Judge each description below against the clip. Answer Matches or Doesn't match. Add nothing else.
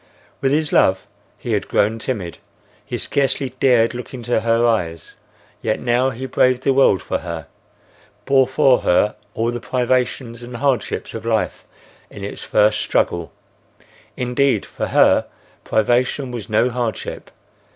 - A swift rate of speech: Doesn't match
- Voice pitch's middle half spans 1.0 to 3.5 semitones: Matches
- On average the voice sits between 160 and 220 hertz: Doesn't match